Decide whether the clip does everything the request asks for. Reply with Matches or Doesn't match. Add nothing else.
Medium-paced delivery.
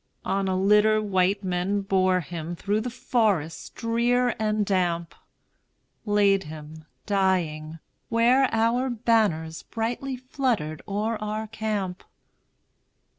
Doesn't match